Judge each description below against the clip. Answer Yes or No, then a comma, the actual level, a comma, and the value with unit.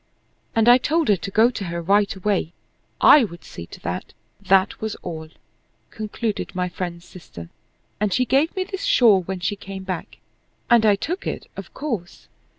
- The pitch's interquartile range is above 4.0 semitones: Yes, average, 4.7 semitones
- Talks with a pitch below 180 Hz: No, high, 200 Hz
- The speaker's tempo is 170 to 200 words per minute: Yes, average, 180 wpm